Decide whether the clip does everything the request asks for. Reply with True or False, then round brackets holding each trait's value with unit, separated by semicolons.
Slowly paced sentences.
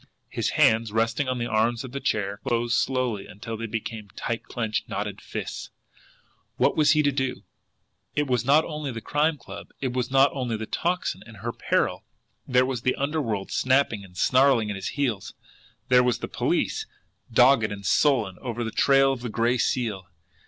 False (190 wpm)